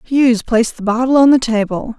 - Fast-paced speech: Yes, fast, 210 wpm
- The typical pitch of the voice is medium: No, high, 240 Hz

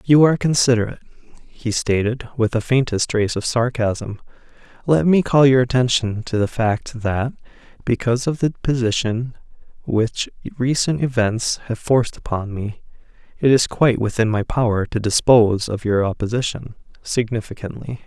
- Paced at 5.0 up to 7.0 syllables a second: Yes, 5.1 syllables/s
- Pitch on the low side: Yes, low, 115 Hz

